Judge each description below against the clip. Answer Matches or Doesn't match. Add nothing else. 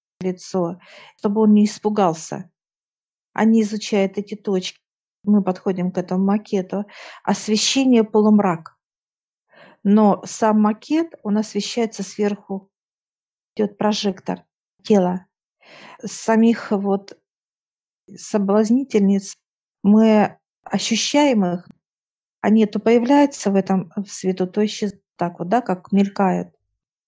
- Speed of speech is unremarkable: Doesn't match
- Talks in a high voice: Matches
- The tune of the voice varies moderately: Doesn't match